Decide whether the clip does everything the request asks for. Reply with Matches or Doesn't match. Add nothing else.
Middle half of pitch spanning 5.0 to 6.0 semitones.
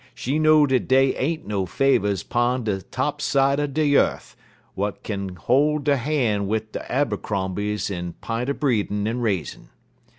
Matches